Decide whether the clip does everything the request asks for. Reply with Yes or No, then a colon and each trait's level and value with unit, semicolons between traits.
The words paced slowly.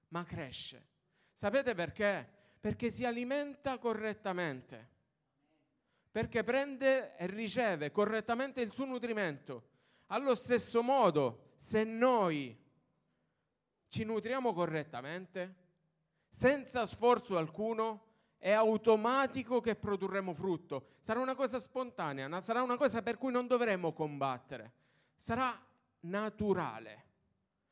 Yes: slow, 100 wpm